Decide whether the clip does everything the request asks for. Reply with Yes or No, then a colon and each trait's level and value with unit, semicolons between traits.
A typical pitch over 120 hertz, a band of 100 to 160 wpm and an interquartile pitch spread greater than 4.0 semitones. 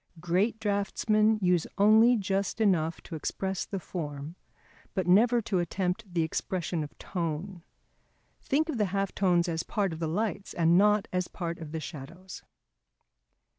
No: medium, 185 Hz; average, 155 wpm; average, 3.6 semitones